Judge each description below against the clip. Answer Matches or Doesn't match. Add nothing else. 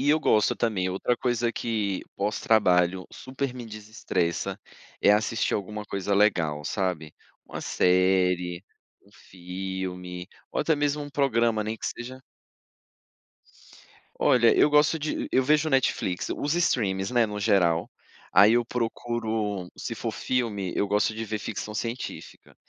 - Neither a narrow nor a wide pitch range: Matches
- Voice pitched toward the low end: Matches